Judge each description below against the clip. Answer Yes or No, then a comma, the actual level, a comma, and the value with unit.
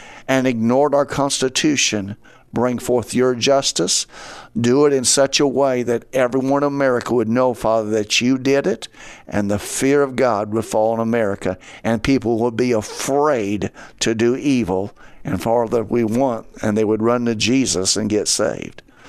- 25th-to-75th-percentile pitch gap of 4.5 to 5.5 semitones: No, average, 3.4 semitones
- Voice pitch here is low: Yes, low, 120 Hz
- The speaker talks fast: No, average, 175 wpm